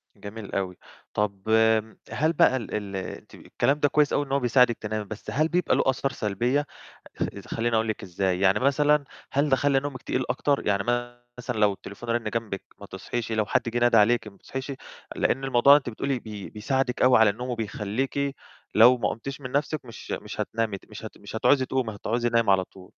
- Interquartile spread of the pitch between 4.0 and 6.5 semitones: Yes, average, 4.3 semitones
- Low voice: Yes, low, 120 Hz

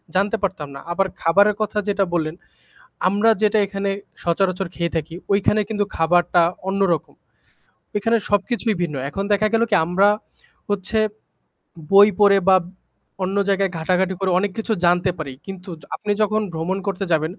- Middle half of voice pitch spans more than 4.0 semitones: No, average, 2.7 semitones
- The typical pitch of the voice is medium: No, high, 195 Hz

